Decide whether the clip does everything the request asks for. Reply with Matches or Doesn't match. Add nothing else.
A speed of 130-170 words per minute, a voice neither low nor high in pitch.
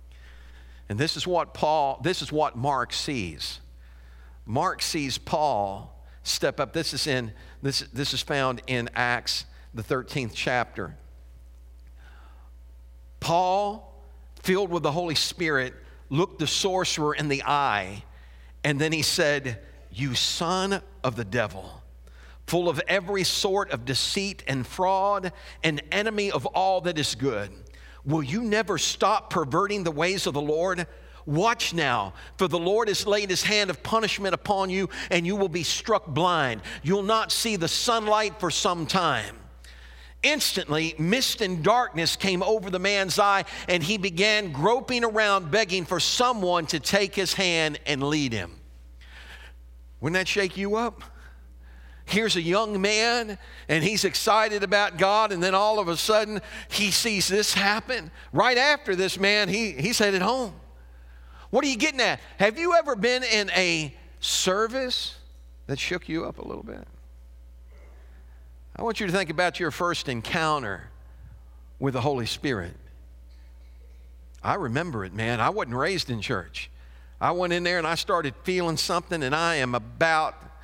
Matches